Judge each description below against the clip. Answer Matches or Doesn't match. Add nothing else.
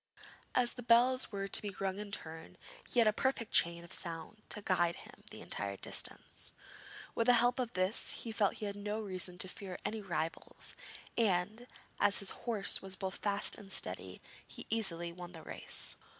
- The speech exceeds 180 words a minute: Matches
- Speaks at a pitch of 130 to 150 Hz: Doesn't match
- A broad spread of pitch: Doesn't match